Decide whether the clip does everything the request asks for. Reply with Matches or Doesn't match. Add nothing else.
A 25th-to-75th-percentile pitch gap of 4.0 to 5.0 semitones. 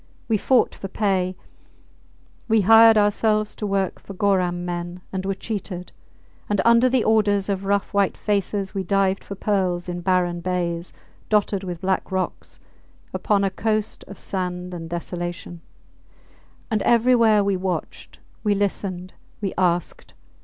Doesn't match